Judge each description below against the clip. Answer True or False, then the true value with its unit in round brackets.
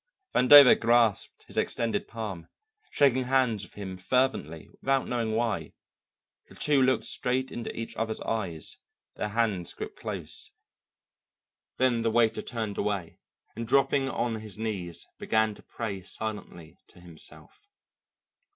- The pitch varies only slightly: False (3.8 semitones)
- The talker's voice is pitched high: False (115 Hz)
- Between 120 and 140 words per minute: True (135 wpm)